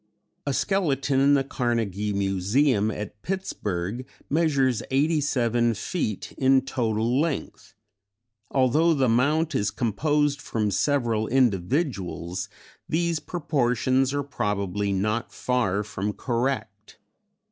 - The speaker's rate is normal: No, slow, 105 wpm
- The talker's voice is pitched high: No, low, 125 Hz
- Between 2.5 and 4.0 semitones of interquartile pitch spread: No, wide, 5.4 semitones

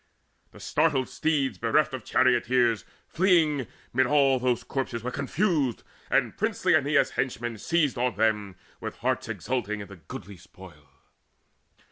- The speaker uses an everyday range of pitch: Yes, average, 4.3 semitones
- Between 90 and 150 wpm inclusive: Yes, slow, 135 wpm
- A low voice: Yes, low, 125 Hz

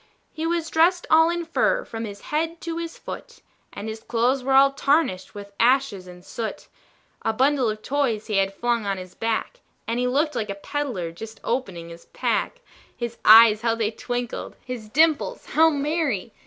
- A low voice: No, high, 240 Hz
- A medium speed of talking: Yes, average, 185 wpm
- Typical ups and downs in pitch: No, wide, 6.0 semitones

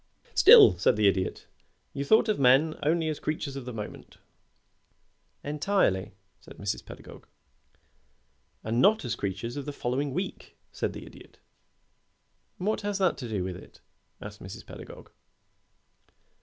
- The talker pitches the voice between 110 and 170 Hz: Yes, low, 135 Hz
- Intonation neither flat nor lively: No, wide, 6.8 semitones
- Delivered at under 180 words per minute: Yes, average, 145 wpm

